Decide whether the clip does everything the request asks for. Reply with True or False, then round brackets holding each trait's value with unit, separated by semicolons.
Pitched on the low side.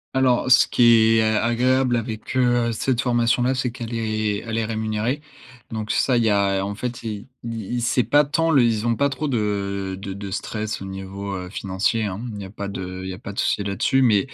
True (110 Hz)